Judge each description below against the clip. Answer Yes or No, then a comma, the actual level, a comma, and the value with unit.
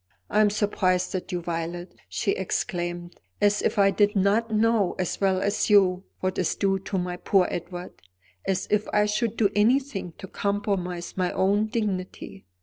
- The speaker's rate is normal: Yes, average, 170 wpm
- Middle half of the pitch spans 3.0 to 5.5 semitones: No, narrow, 2.5 semitones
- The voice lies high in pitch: Yes, high, 195 Hz